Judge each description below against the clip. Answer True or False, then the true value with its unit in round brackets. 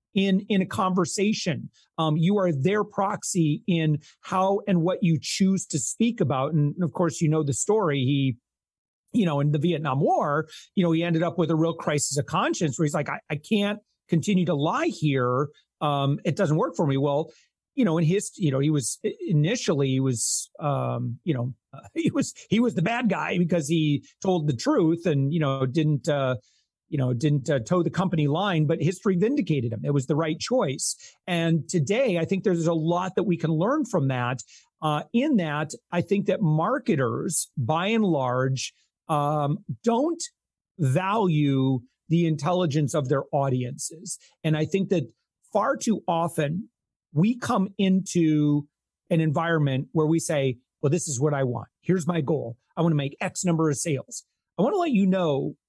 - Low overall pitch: False (165 Hz)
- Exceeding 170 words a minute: True (190 wpm)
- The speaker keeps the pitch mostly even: False (4.4 semitones)